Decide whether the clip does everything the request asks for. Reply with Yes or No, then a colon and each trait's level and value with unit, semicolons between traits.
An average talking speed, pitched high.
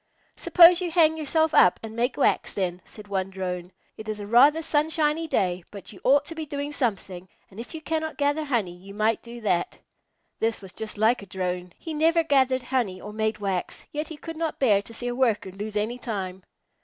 No: fast, 215 wpm; high, 230 Hz